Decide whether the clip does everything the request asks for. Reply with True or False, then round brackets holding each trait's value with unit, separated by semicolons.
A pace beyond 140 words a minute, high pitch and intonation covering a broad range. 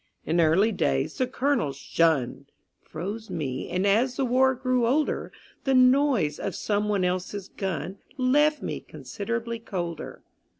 False (135 wpm; 210 Hz; 6.9 semitones)